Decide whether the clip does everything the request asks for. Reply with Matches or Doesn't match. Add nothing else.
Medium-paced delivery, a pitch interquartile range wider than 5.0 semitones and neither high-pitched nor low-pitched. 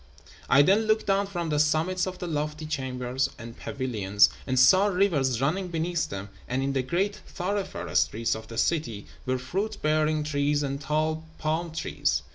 Matches